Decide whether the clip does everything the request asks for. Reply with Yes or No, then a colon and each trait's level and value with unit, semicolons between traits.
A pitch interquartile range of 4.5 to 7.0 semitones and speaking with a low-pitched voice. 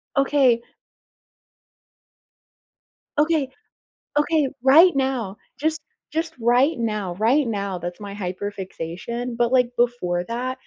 No: average, 5.3 semitones; high, 240 Hz